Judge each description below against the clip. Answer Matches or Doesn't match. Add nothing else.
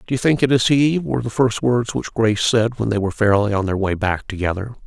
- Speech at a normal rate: Doesn't match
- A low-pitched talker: Matches